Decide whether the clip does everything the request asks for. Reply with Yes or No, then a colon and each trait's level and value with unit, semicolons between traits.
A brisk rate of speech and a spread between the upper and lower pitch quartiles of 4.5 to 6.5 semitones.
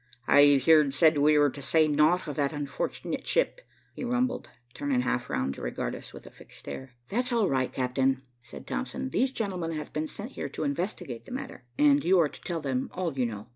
Yes: fast, 215 wpm; average, 5.3 semitones